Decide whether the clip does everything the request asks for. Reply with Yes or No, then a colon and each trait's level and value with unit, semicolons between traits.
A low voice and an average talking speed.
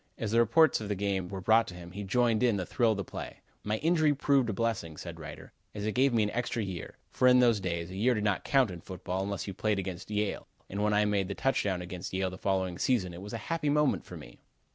No: low, 105 Hz; fast, 270 wpm